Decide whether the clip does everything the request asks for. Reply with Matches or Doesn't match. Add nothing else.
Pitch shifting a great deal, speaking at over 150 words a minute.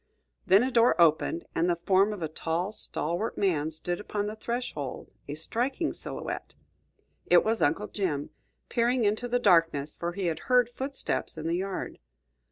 Matches